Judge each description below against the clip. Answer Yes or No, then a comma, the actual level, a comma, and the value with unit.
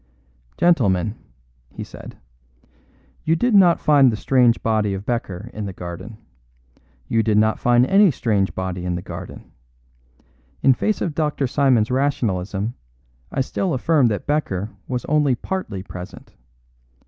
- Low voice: Yes, low, 120 Hz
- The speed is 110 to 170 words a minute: Yes, average, 140 wpm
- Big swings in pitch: Yes, wide, 6.4 semitones